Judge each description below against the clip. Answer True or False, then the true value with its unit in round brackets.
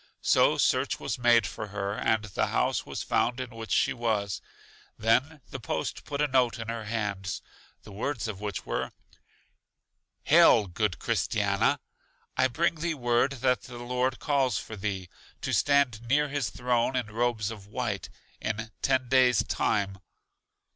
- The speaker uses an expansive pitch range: False (3.5 semitones)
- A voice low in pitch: True (120 Hz)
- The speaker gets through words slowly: False (160 wpm)